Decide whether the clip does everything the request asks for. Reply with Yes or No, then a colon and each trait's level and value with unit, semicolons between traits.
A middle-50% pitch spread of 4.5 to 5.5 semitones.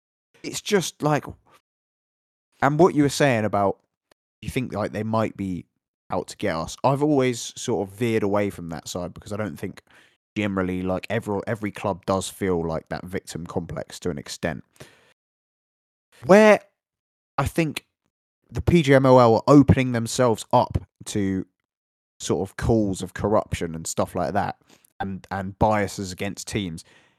Yes: average, 5.1 semitones